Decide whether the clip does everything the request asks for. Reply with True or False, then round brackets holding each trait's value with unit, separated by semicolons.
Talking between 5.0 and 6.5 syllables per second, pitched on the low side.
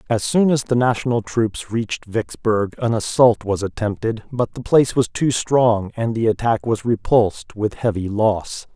False (4.6 syllables/s; 115 Hz)